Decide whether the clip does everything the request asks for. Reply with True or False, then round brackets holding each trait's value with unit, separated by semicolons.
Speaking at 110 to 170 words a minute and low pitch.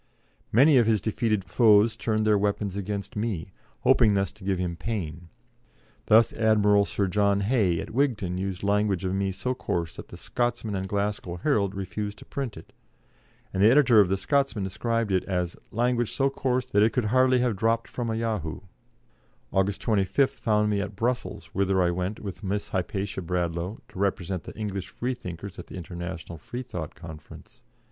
False (180 wpm; 100 Hz)